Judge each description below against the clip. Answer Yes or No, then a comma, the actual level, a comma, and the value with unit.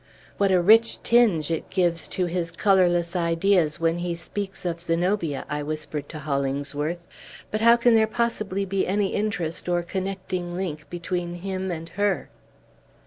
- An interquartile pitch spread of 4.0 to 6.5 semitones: No, average, 2.9 semitones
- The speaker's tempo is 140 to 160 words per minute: Yes, average, 155 wpm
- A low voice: No, medium, 175 Hz